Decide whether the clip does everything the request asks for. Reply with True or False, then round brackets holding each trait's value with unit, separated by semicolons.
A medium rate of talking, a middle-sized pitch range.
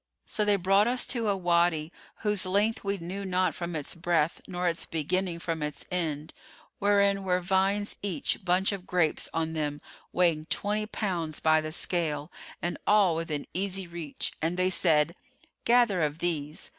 True (170 wpm; 3.4 semitones)